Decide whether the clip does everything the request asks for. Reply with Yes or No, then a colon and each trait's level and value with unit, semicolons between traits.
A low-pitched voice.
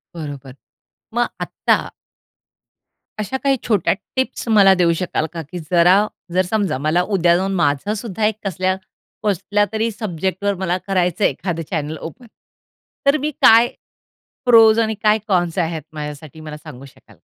No: medium, 185 Hz